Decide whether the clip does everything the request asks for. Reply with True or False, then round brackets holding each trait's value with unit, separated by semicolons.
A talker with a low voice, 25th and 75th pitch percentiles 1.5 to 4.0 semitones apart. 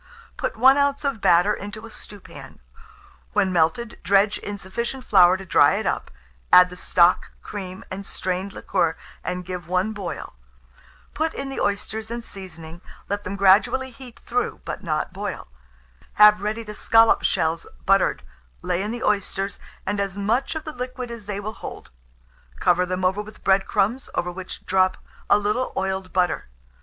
False (200 Hz; 3.4 semitones)